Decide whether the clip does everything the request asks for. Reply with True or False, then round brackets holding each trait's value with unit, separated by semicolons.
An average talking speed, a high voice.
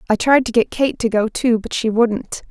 False (265 wpm; 230 Hz)